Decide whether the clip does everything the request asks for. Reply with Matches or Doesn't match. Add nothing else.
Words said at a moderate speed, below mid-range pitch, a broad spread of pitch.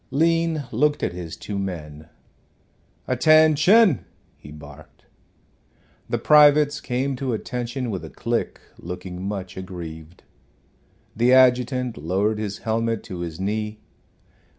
Doesn't match